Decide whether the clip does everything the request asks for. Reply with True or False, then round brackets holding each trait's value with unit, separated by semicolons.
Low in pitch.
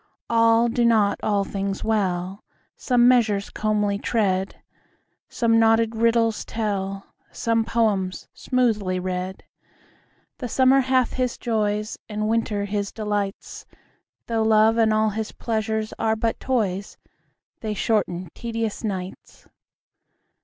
False (220 Hz)